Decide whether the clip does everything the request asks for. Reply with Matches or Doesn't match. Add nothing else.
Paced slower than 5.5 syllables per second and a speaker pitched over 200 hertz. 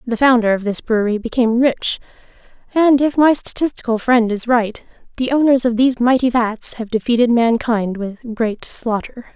Matches